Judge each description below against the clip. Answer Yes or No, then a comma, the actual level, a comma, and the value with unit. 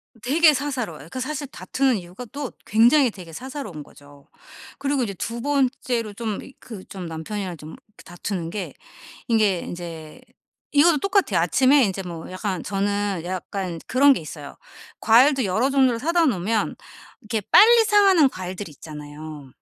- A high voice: Yes, high, 215 Hz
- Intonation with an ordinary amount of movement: No, wide, 7.4 semitones